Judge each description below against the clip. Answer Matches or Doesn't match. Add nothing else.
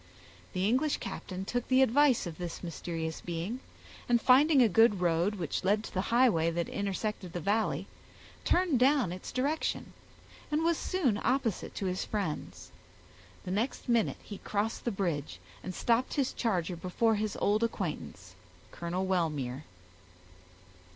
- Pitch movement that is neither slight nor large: Doesn't match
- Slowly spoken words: Doesn't match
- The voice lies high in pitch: Matches